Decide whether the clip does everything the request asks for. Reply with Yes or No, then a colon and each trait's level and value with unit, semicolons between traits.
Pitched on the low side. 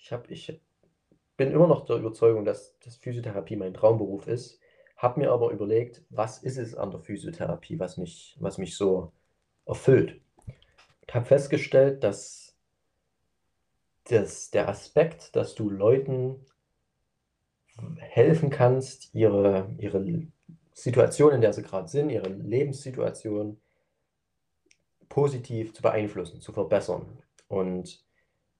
Yes: low, 120 Hz